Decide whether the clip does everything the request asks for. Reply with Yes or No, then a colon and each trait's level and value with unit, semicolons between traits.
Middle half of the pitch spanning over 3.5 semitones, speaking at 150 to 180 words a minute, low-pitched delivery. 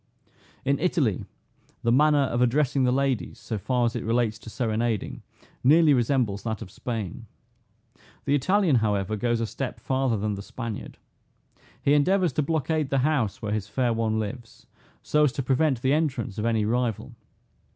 Yes: average, 4.1 semitones; average, 170 wpm; low, 125 Hz